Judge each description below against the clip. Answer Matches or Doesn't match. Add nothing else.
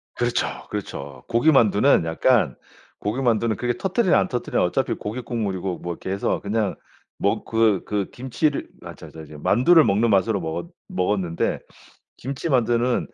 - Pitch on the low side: Matches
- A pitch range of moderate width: Matches